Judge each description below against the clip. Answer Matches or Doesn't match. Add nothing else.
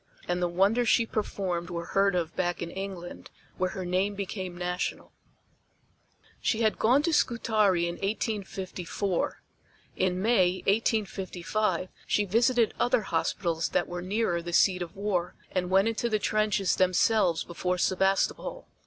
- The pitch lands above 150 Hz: Matches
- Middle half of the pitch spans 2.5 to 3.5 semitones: Matches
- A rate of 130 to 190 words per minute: Matches